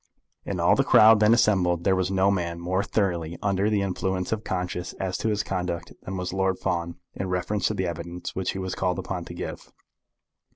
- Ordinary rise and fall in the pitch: No, narrow, 1.8 semitones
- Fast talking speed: Yes, fast, 210 wpm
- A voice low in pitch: Yes, very low, 95 Hz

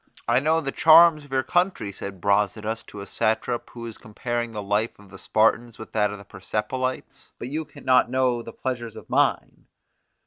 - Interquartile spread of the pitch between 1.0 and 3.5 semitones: No, average, 3.9 semitones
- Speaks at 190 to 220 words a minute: Yes, average, 200 wpm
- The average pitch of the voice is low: Yes, low, 115 Hz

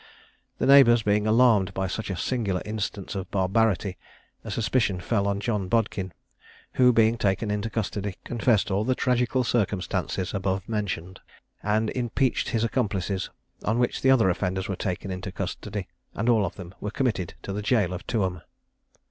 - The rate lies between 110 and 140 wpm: No, average, 165 wpm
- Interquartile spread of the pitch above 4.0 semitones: No, average, 3.3 semitones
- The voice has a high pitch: No, low, 105 Hz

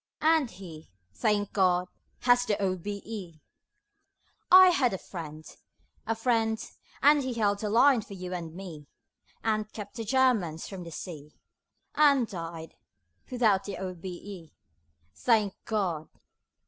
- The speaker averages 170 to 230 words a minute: No, slow, 135 wpm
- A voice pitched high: Yes, high, 200 Hz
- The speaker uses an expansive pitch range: No, average, 4.5 semitones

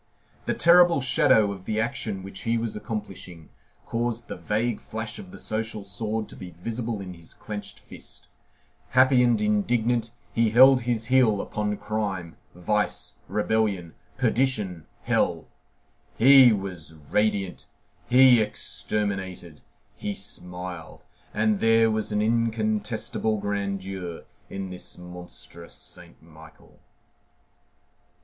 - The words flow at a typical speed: No, slow, 120 wpm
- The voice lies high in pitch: No, low, 105 Hz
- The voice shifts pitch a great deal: No, average, 3.2 semitones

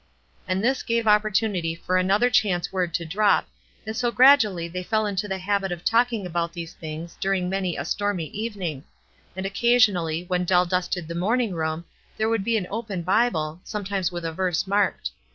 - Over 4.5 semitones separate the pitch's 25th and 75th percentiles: No, average, 3.7 semitones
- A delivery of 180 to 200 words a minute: Yes, average, 190 wpm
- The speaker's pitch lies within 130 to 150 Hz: No, high, 190 Hz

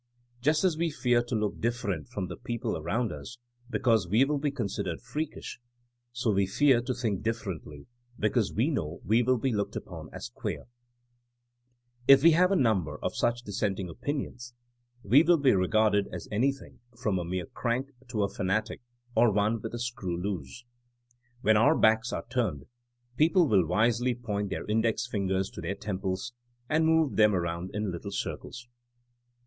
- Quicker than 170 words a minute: Yes, average, 180 wpm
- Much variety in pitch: No, average, 4.2 semitones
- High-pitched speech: No, low, 115 Hz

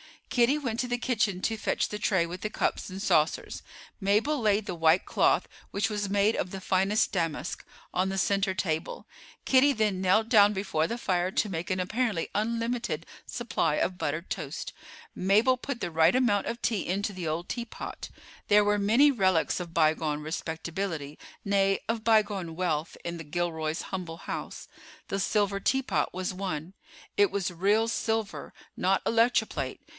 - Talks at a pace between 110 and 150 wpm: No, average, 165 wpm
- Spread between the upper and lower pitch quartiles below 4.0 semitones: No, average, 4.3 semitones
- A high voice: Yes, high, 195 Hz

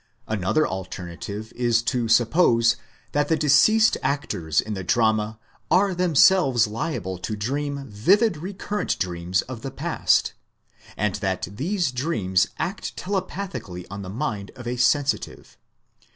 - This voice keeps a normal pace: No, slow, 130 wpm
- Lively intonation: Yes, wide, 7.3 semitones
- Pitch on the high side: No, low, 120 Hz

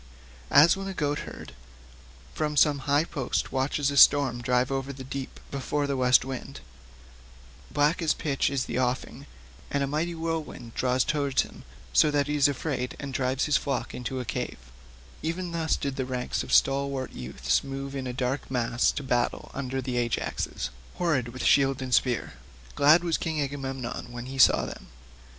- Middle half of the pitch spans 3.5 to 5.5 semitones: No, narrow, 2.6 semitones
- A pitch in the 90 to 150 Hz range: Yes, low, 135 Hz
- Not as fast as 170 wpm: No, average, 175 wpm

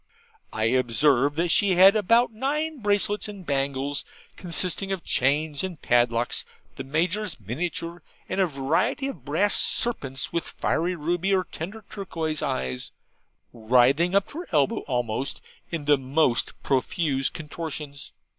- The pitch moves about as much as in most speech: No, wide, 6.1 semitones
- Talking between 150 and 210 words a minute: No, slow, 135 wpm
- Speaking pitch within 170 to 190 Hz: No, medium, 160 Hz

